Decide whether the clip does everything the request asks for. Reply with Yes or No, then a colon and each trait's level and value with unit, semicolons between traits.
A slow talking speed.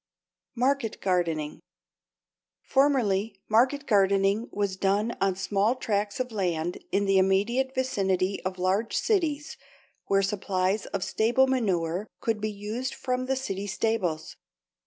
Yes: slow, 125 wpm